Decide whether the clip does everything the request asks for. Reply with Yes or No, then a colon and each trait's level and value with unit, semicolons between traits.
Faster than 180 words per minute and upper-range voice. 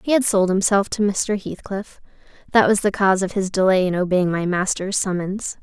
Yes: fast, 205 wpm; high, 195 Hz